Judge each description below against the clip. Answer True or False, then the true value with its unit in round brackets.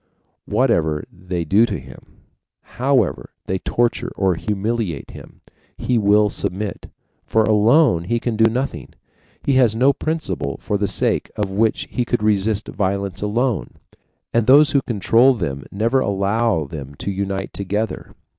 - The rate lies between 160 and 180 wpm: False (145 wpm)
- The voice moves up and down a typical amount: True (3.5 semitones)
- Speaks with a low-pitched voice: True (105 Hz)